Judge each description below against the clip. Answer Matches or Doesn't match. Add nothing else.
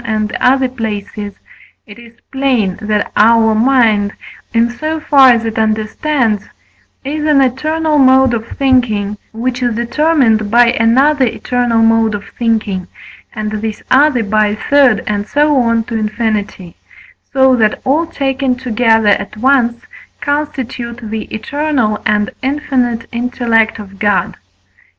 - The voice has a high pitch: Matches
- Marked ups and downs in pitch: Doesn't match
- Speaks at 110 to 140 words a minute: Matches